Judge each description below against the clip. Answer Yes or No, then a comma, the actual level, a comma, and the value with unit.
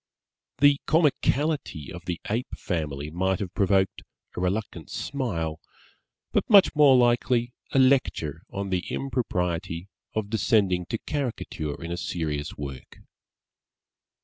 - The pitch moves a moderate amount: No, wide, 7.1 semitones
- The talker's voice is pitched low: Yes, very low, 95 Hz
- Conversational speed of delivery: No, slow, 120 wpm